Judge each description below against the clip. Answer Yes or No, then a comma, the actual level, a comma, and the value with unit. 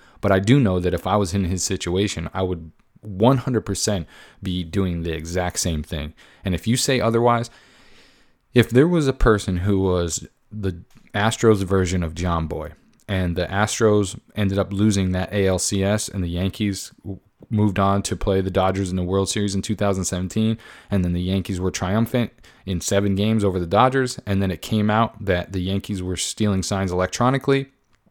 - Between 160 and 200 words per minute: Yes, average, 180 wpm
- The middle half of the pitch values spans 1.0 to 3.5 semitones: Yes, average, 2.9 semitones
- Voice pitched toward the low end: Yes, low, 100 Hz